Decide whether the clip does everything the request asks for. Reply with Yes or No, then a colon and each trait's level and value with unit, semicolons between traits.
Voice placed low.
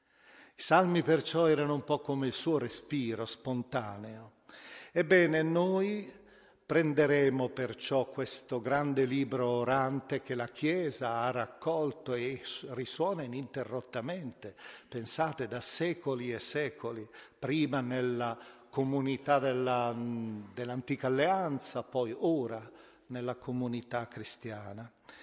Yes: low, 130 Hz